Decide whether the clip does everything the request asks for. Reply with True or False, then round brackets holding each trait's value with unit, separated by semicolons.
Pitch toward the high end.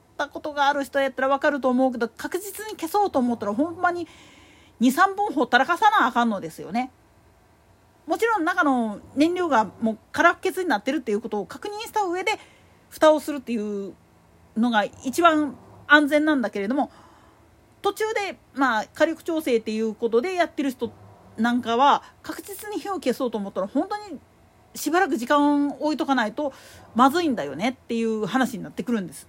True (280 Hz)